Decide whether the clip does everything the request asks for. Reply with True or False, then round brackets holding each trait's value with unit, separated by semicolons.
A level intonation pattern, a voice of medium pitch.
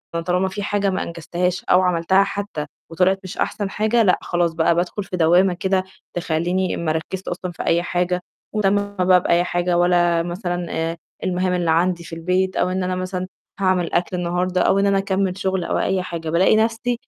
True (1.7 semitones; 180 Hz)